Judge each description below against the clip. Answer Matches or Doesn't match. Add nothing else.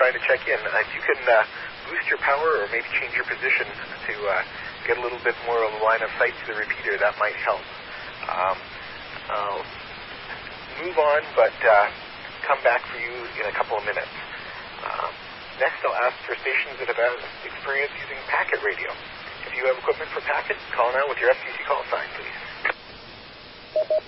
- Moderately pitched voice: Matches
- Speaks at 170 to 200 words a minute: Matches